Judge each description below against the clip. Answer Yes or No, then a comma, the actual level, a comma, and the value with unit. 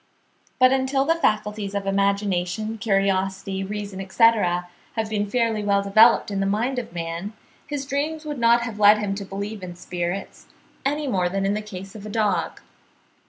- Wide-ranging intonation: No, average, 2.9 semitones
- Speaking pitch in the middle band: No, high, 205 Hz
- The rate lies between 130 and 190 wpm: Yes, average, 175 wpm